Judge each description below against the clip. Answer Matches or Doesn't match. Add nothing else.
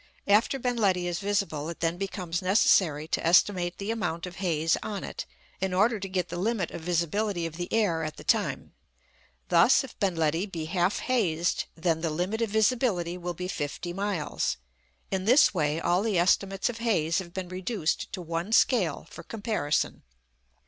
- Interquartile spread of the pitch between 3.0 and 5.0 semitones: Matches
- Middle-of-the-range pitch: Matches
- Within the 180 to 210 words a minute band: Matches